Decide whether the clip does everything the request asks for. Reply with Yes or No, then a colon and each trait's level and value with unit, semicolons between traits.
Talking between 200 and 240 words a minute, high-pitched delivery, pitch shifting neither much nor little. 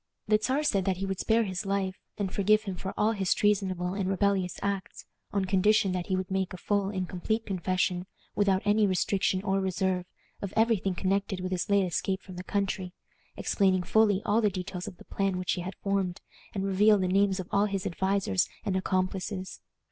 No: fast, 205 wpm; high, 195 Hz; narrow, 1.5 semitones